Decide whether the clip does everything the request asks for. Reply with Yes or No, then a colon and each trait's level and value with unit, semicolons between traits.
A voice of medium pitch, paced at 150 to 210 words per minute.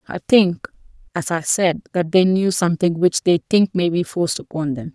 Yes: medium, 175 Hz; fast, 205 wpm